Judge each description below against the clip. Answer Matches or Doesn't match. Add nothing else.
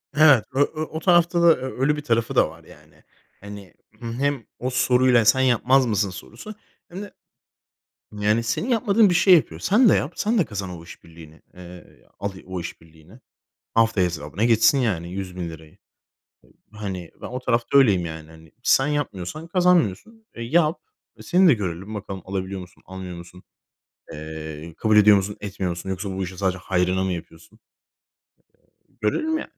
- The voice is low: Matches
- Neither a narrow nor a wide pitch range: Doesn't match